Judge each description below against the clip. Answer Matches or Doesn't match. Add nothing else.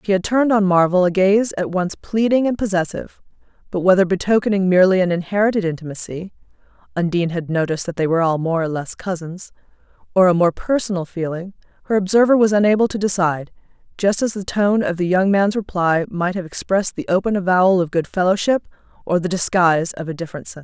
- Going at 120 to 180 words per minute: Doesn't match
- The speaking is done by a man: Doesn't match